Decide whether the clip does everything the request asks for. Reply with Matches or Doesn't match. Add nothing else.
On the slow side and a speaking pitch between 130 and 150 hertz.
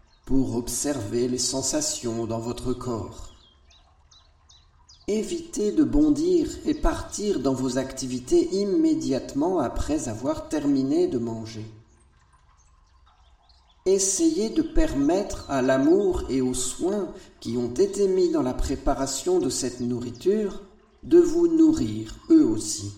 Matches